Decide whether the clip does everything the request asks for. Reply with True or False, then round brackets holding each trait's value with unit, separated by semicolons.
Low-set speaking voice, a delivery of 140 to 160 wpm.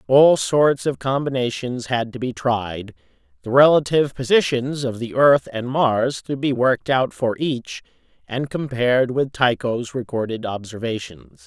True (125 Hz; 145 wpm)